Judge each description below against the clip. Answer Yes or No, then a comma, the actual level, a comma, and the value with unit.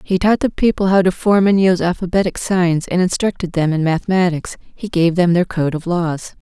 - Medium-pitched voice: Yes, medium, 180 Hz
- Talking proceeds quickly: Yes, fast, 215 wpm